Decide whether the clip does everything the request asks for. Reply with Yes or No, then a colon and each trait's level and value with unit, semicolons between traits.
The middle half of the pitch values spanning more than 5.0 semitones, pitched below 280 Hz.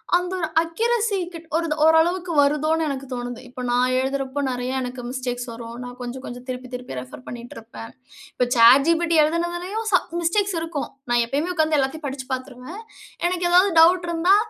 No: wide, 5.5 semitones; very high, 285 Hz